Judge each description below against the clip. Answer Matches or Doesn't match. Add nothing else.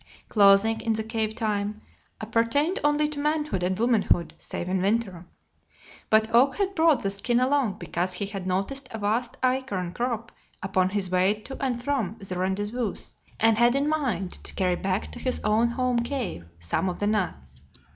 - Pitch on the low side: Doesn't match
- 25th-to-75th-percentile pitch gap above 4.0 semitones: Matches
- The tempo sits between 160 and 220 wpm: Matches